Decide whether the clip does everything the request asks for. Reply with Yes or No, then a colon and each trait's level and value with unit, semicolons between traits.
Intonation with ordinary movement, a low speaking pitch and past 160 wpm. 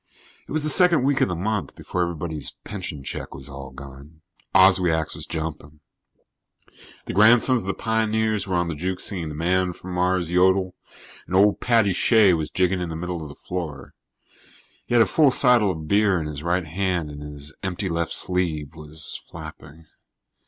Yes: average, 4.1 semitones; very low, 90 Hz; average, 185 wpm